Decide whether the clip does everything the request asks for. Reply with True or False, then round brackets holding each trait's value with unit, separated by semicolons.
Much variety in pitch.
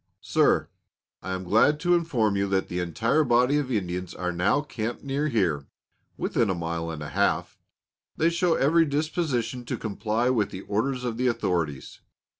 True (7.5 semitones)